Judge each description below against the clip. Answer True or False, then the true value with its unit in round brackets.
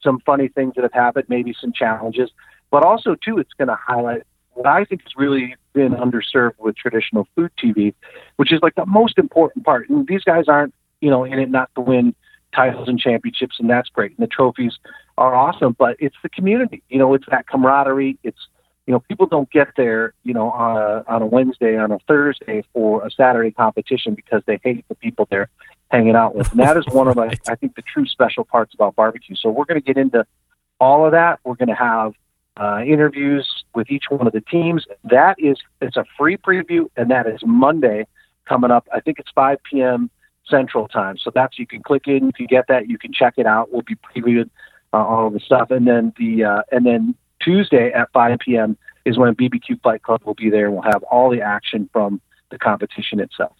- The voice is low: True (125 Hz)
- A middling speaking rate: False (220 wpm)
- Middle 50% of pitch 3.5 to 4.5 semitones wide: True (4.2 semitones)